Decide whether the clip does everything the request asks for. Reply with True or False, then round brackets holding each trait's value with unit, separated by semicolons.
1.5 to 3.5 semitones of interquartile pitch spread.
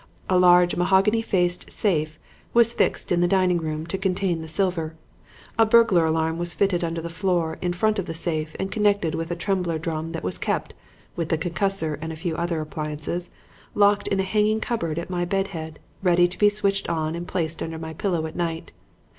True (3.0 semitones)